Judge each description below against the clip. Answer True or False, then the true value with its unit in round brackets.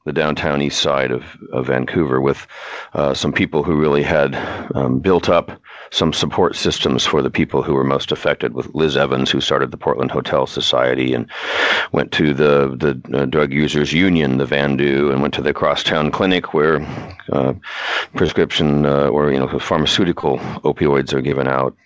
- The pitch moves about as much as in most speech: False (1.5 semitones)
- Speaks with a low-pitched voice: True (70 Hz)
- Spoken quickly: False (180 wpm)